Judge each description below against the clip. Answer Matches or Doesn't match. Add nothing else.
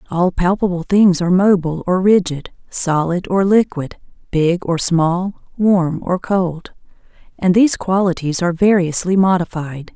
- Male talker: Doesn't match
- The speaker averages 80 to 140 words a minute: Matches